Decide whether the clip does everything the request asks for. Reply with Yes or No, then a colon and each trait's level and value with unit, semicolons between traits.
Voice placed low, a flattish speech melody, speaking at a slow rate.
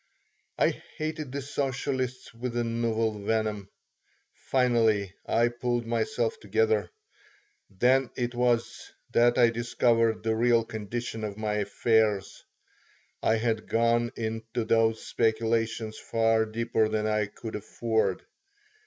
Yes: low, 115 Hz; narrow, 1.6 semitones; slow, 120 wpm